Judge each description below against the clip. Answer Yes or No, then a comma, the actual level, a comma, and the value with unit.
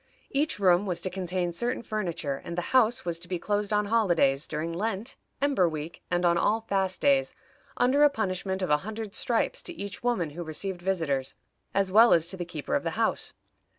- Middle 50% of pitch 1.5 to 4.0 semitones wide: No, average, 4.4 semitones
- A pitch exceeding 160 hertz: Yes, high, 190 Hz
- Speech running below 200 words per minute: No, fast, 205 wpm